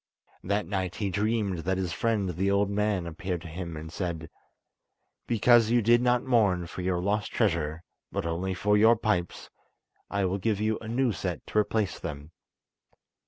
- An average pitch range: Yes, average, 3.6 semitones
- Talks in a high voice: No, low, 100 Hz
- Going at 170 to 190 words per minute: Yes, average, 175 wpm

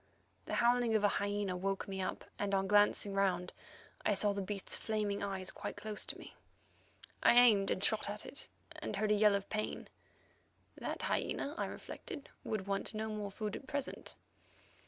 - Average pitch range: No, narrow, 1.6 semitones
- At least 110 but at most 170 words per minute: No, average, 180 wpm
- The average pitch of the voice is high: Yes, high, 205 Hz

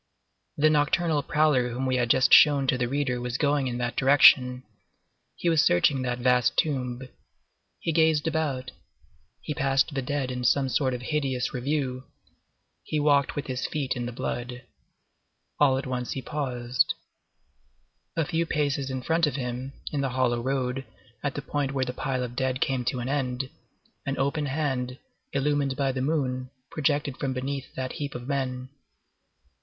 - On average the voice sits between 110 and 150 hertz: Yes, low, 135 Hz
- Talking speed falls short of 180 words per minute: Yes, average, 170 wpm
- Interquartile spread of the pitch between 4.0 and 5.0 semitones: No, narrow, 2.4 semitones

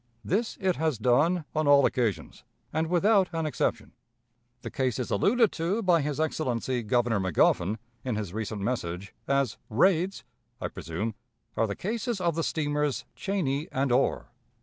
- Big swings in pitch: Yes, wide, 6.9 semitones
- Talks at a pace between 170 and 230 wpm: No, average, 150 wpm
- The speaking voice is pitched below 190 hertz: Yes, medium, 140 Hz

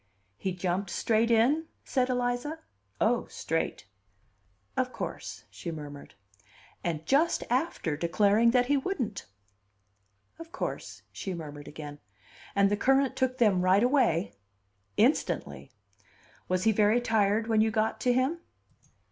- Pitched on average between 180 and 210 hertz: No, high, 220 Hz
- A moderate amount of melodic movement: No, wide, 5.9 semitones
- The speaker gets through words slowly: Yes, slow, 130 wpm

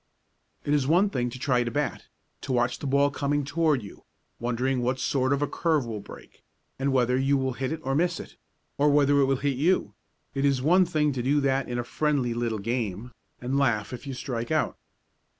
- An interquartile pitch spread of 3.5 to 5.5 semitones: No, average, 2.9 semitones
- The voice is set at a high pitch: No, low, 135 Hz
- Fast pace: Yes, fast, 220 wpm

